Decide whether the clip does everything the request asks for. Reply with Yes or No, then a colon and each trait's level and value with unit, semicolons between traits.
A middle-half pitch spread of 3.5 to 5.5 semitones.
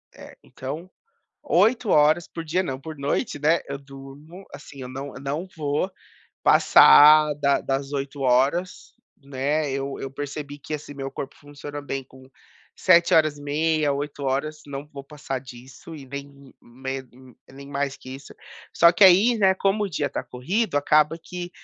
No: average, 2.7 semitones